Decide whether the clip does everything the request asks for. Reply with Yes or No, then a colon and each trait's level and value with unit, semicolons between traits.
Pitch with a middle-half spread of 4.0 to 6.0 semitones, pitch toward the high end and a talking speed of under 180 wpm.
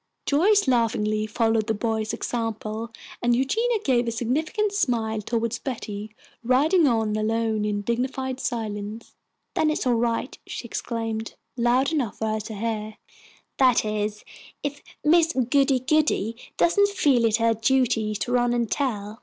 No: average, 3.4 semitones; high, 235 Hz; average, 150 wpm